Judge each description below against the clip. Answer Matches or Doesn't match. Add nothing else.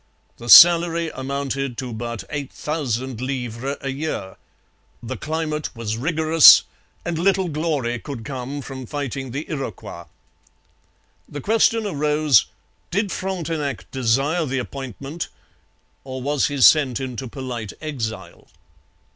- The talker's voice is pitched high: Doesn't match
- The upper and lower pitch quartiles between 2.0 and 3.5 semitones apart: Doesn't match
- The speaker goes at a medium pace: Doesn't match